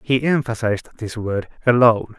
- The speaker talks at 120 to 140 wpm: Yes, slow, 135 wpm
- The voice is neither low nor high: No, low, 115 Hz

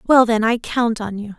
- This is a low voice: No, high, 225 Hz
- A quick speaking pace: Yes, fast, 260 wpm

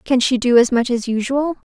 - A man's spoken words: No, female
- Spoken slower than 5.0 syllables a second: No, 5.4 syllables/s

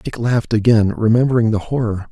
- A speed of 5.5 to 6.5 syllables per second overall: Yes, 6.0 syllables/s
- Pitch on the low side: Yes, low, 115 Hz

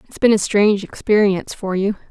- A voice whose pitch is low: No, high, 205 Hz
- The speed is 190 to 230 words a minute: Yes, average, 200 wpm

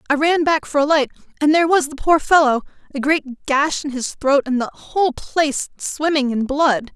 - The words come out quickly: Yes, fast, 215 wpm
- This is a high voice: Yes, very high, 290 Hz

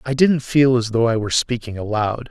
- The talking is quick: Yes, fast, 235 wpm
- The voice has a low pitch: Yes, low, 120 Hz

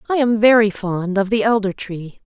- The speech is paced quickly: Yes, fast, 210 wpm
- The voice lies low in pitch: No, high, 210 Hz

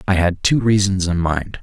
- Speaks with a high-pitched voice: No, very low, 95 Hz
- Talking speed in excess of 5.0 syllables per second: No, 4.7 syllables/s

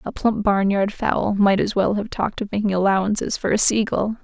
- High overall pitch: Yes, high, 205 Hz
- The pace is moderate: No, fast, 215 wpm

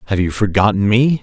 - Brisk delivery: No, average, 195 wpm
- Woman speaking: No, male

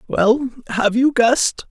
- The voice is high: Yes, high, 240 Hz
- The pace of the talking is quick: No, average, 140 wpm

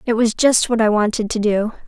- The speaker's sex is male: No, female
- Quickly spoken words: Yes, fast, 255 wpm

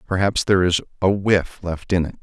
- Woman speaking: No, male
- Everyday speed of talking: No, fast, 215 wpm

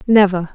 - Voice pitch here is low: No, high, 195 Hz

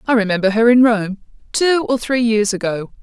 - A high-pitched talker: Yes, high, 225 Hz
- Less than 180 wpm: No, average, 200 wpm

